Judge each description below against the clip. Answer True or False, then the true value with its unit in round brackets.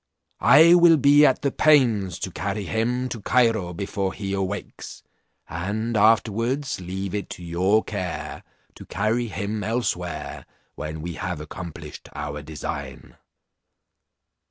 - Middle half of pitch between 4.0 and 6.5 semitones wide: True (4.9 semitones)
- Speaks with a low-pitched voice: True (100 Hz)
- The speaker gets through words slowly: True (130 wpm)